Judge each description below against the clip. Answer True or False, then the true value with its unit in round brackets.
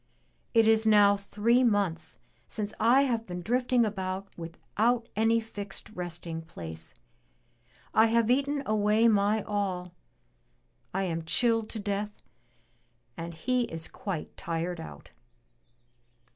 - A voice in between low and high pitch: False (205 Hz)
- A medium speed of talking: False (120 wpm)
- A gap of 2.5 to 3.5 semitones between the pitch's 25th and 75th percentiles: False (4.2 semitones)